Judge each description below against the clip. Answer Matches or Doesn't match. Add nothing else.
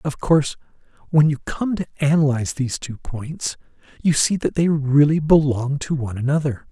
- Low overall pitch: Doesn't match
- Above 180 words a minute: Doesn't match